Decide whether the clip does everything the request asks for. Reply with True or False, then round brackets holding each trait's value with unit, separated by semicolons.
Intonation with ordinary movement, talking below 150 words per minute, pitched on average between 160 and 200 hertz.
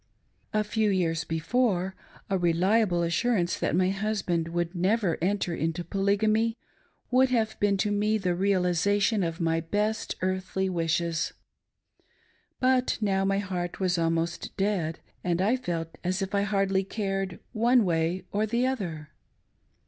True (3.5 semitones; 140 wpm; 190 Hz)